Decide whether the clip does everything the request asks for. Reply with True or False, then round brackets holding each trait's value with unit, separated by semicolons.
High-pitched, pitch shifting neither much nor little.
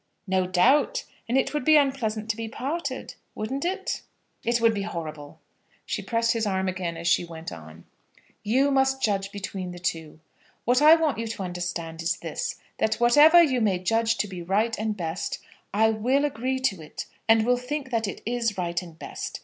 False (220 Hz; 6.3 semitones)